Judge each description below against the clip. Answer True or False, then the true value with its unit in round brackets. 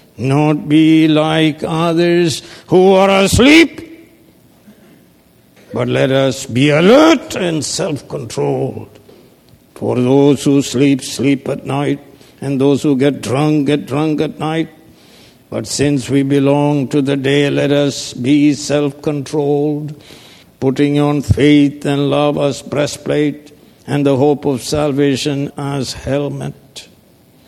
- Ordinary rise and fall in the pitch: False (1.6 semitones)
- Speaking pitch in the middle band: True (145 Hz)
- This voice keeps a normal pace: False (125 wpm)